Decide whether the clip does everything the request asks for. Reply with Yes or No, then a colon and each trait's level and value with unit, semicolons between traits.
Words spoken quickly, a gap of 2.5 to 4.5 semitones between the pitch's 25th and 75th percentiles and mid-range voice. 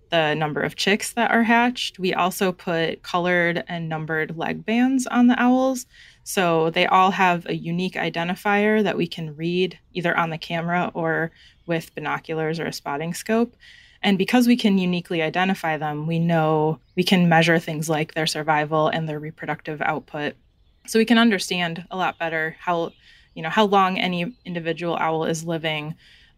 No: average, 175 wpm; average, 3.3 semitones; medium, 175 Hz